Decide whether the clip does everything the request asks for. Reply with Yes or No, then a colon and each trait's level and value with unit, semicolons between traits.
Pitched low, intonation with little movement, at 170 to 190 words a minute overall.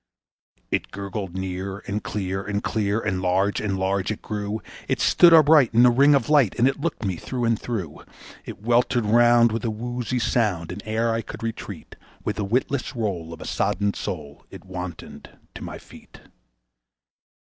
No: low, 105 Hz; average, 3.9 semitones; average, 180 wpm